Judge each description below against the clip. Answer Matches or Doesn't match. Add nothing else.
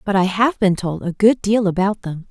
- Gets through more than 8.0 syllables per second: Doesn't match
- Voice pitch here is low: Doesn't match